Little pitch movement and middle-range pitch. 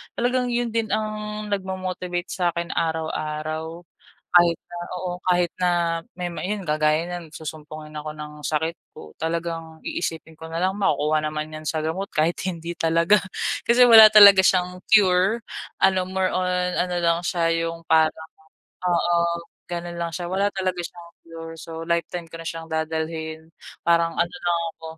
Yes: narrow, 2.2 semitones; medium, 170 Hz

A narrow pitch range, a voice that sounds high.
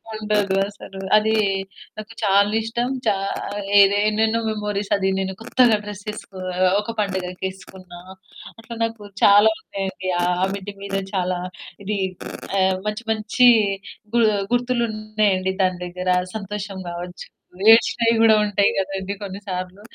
Yes: narrow, 2.2 semitones; high, 205 Hz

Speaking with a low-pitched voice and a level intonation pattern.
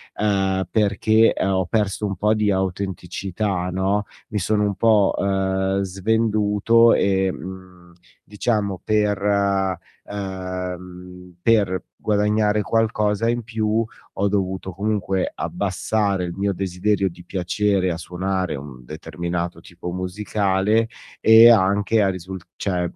Yes: very low, 95 Hz; narrow, 2.3 semitones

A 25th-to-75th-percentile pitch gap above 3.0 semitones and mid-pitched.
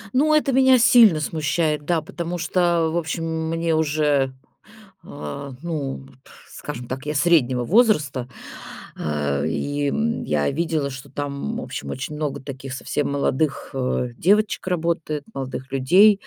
Yes: average, 4.1 semitones; medium, 150 Hz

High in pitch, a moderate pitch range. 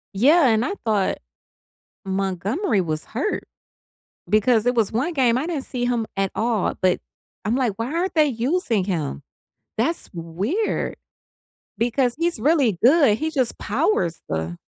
No: high, 235 Hz; wide, 6.5 semitones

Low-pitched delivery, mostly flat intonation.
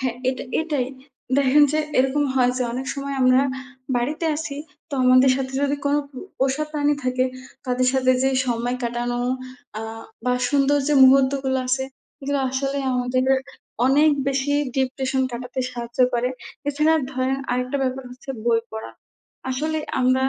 No: very high, 265 Hz; narrow, 1.7 semitones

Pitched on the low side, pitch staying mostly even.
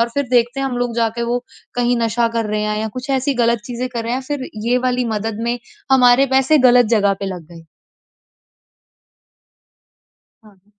No: high, 240 Hz; narrow, 2.3 semitones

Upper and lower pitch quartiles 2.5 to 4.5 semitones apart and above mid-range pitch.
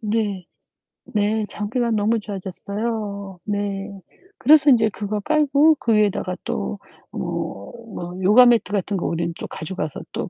Yes: average, 2.9 semitones; high, 205 Hz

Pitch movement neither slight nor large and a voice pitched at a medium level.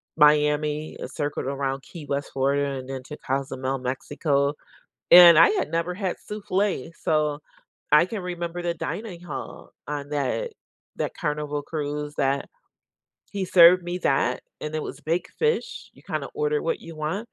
Yes: average, 3.9 semitones; medium, 150 Hz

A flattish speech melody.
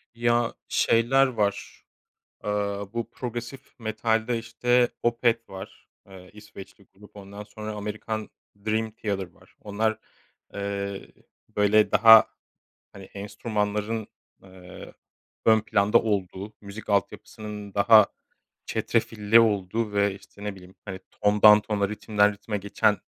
Yes: narrow, 1.8 semitones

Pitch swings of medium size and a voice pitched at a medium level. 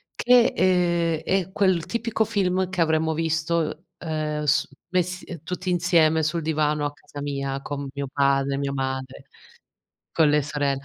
Yes: average, 3.8 semitones; medium, 160 Hz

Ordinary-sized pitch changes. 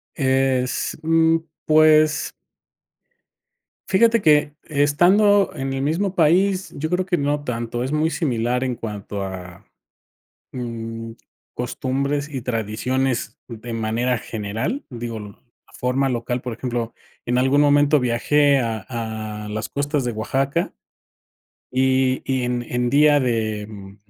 Yes: average, 4.2 semitones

